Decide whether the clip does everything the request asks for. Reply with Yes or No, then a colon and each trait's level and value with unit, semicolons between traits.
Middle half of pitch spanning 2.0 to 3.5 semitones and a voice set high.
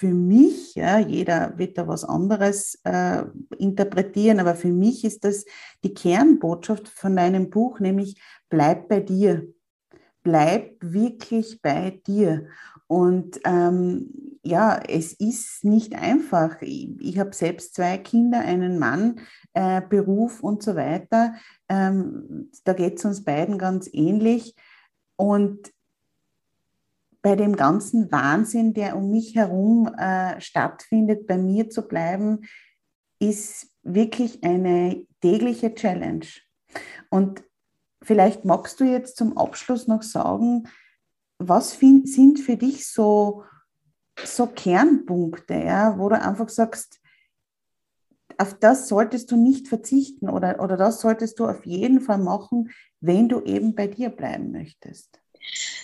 No: average, 4.1 semitones; high, 210 Hz